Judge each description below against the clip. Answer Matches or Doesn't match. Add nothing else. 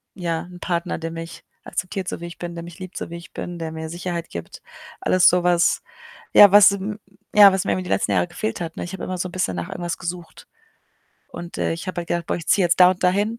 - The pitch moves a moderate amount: Doesn't match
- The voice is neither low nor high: Matches